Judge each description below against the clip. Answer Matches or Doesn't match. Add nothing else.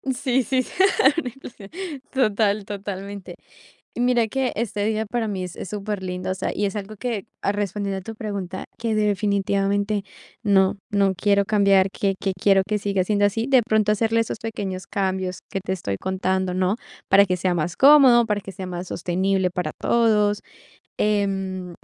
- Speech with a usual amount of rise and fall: Doesn't match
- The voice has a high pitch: Matches